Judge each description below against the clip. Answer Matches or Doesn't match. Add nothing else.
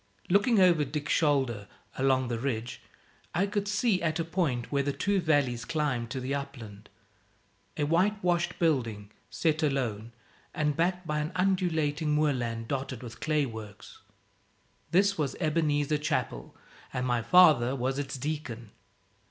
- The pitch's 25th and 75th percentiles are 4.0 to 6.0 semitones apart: Matches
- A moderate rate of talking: Matches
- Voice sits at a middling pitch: Matches